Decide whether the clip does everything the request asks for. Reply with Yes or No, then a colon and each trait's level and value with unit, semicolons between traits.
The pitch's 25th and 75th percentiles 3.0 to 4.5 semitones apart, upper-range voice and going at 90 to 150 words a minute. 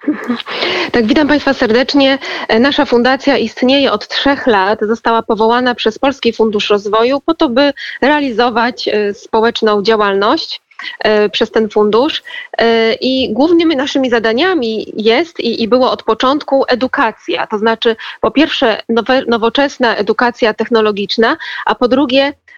Yes: average, 3.8 semitones; high, 245 Hz; average, 120 wpm